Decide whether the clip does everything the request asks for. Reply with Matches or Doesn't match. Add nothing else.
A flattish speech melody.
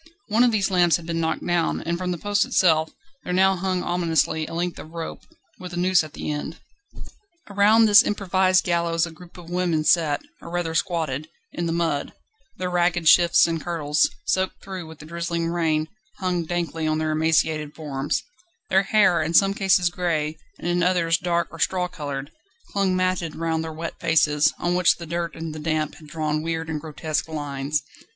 Matches